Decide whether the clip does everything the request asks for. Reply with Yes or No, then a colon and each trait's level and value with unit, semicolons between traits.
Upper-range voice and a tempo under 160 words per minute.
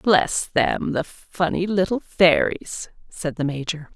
No: medium, 170 Hz; slow, 135 wpm